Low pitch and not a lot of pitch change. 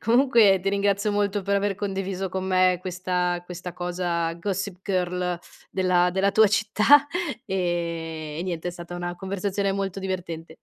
No: medium, 185 Hz; narrow, 2.0 semitones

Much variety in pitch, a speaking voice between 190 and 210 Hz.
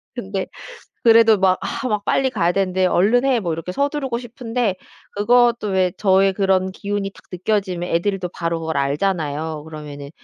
No: average, 4.5 semitones; high, 195 Hz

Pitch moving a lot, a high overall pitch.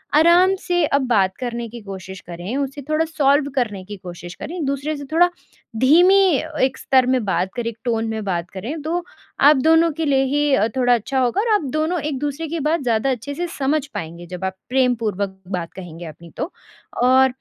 Yes: wide, 7.1 semitones; very high, 260 Hz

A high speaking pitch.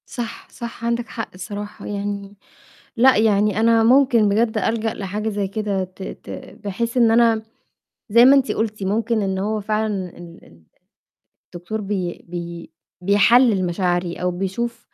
Yes: high, 210 Hz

